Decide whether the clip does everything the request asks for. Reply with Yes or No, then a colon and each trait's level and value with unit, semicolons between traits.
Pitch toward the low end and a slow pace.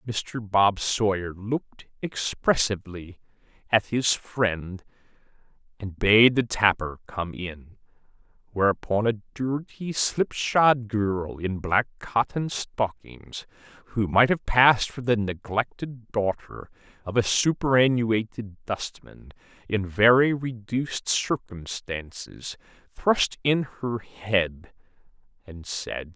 Yes: low, 110 Hz; slow, 105 wpm